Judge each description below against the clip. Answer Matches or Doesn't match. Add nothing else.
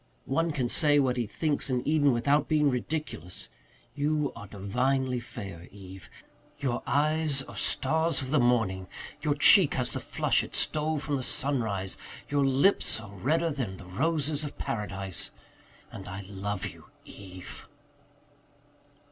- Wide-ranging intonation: Matches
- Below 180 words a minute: Matches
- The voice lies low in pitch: Matches